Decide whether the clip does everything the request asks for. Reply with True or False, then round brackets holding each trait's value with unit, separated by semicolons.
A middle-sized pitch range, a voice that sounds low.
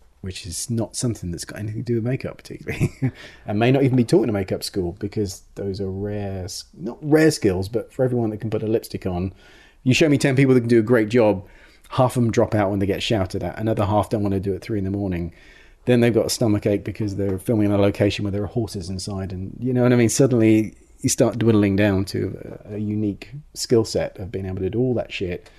True (3.4 semitones; 105 Hz)